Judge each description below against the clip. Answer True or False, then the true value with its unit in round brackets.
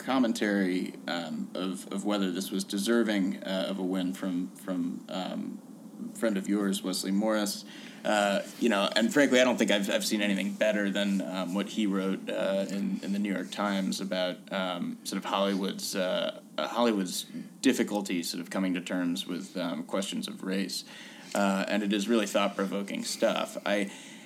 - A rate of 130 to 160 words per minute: False (180 wpm)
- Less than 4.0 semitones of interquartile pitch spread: True (2.7 semitones)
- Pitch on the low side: True (100 Hz)